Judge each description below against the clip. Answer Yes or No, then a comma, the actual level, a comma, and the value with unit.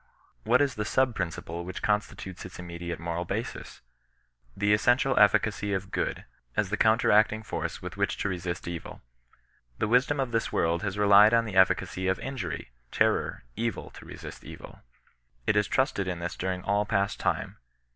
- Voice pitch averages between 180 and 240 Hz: No, low, 100 Hz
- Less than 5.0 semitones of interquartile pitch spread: Yes, average, 3.6 semitones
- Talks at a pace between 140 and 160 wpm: No, average, 175 wpm